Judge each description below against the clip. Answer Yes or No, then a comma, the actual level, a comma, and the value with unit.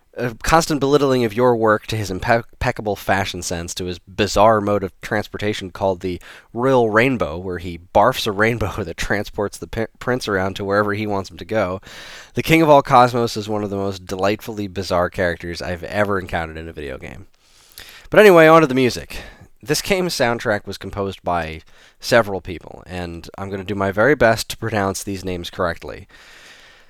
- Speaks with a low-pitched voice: Yes, low, 100 Hz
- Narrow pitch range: No, average, 3.9 semitones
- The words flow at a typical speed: Yes, average, 190 wpm